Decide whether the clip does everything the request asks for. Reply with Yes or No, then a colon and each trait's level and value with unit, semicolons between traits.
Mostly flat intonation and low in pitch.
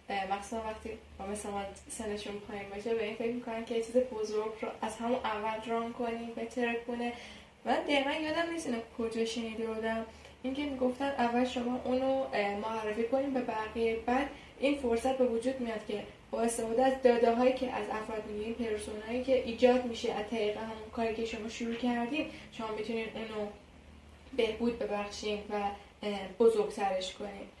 No: narrow, 2.3 semitones; high, 230 Hz